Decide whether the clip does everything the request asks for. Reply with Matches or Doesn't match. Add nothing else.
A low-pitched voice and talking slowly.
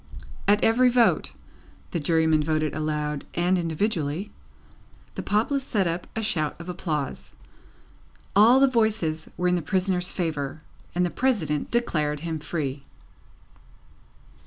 Doesn't match